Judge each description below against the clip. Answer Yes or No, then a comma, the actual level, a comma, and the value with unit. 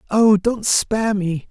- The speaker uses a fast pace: No, average, 160 wpm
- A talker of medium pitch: No, high, 205 Hz